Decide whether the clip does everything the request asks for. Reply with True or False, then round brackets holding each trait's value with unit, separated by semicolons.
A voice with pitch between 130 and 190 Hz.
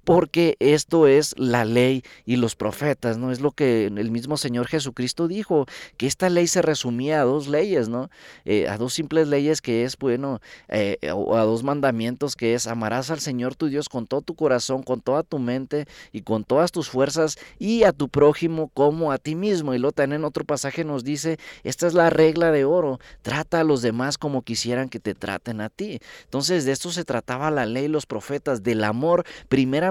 True (140 Hz)